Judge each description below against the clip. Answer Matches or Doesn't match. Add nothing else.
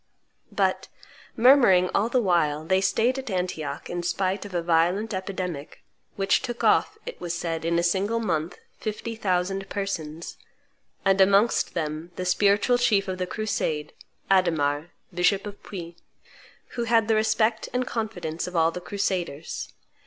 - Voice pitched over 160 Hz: Matches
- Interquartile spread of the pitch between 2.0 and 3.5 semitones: Doesn't match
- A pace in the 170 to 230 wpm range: Doesn't match